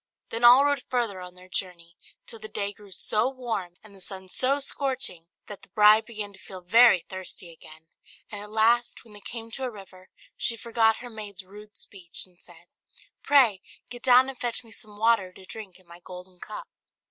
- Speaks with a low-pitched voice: No, high, 210 Hz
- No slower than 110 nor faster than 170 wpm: No, fast, 205 wpm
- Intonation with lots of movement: No, average, 4.1 semitones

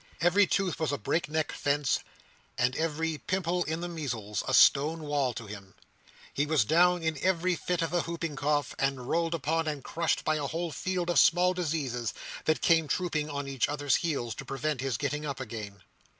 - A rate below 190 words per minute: No, average, 195 wpm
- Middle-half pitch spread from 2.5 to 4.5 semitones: Yes, average, 3.5 semitones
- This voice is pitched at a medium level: Yes, medium, 155 Hz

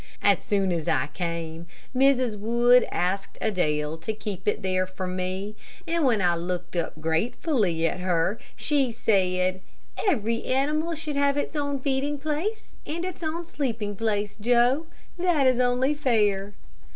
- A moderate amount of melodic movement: No, wide, 7.2 semitones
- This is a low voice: No, high, 220 Hz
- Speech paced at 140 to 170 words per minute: Yes, average, 150 wpm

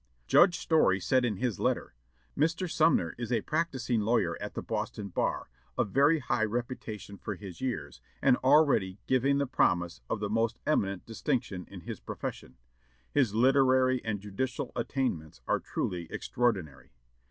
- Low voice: Yes, low, 120 Hz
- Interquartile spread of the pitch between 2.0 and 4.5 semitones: No, average, 5.2 semitones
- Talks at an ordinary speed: Yes, average, 155 wpm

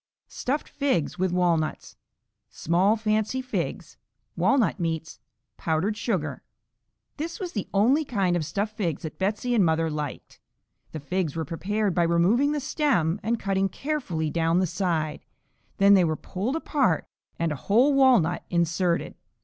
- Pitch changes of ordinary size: No, wide, 5.9 semitones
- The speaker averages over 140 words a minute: Yes, average, 150 wpm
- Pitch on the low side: No, high, 190 Hz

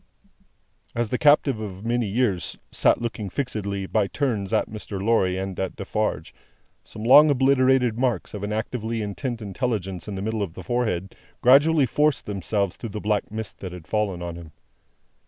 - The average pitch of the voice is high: No, low, 110 Hz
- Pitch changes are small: No, average, 4.1 semitones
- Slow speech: No, average, 175 wpm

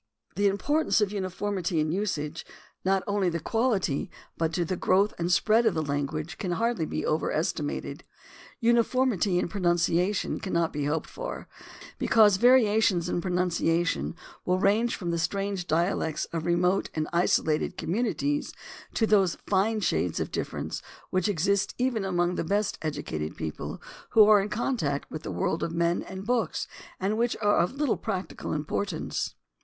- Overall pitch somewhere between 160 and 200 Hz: Yes, medium, 185 Hz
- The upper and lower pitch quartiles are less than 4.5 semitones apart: Yes, average, 4.0 semitones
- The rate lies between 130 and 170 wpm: Yes, average, 160 wpm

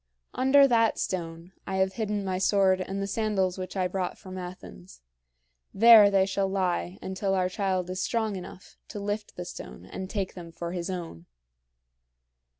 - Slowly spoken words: No, average, 170 wpm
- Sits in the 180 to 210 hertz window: Yes, high, 190 Hz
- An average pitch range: No, narrow, 1.9 semitones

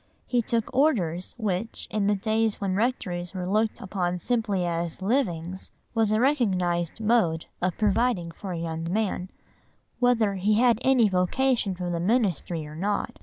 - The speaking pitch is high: Yes, high, 200 Hz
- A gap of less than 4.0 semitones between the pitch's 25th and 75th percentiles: No, average, 4.3 semitones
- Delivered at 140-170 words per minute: Yes, average, 160 wpm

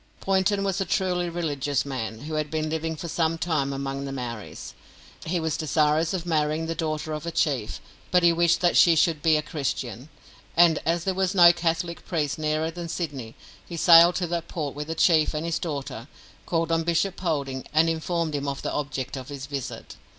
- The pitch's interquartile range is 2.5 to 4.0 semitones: Yes, average, 2.8 semitones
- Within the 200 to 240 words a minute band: Yes, fast, 205 wpm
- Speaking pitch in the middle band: Yes, medium, 160 Hz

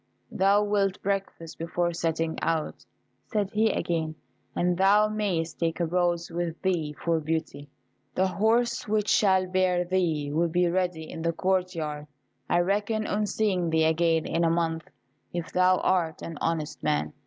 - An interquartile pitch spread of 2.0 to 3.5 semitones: Yes, average, 2.8 semitones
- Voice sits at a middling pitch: Yes, medium, 175 Hz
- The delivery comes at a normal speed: Yes, average, 165 wpm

